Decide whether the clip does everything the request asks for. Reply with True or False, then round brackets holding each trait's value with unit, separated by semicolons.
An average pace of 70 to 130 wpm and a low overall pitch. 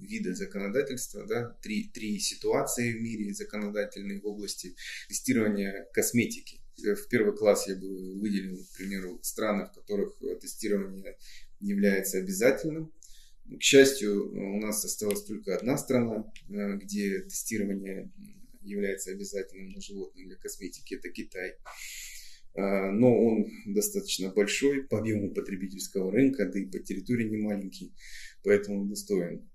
True (125 wpm; 105 Hz)